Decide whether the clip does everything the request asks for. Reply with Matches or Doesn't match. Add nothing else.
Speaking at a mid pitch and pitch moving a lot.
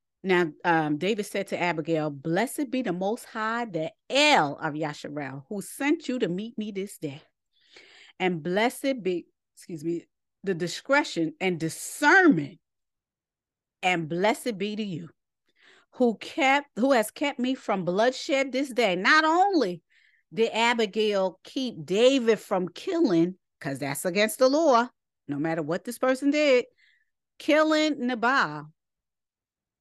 Doesn't match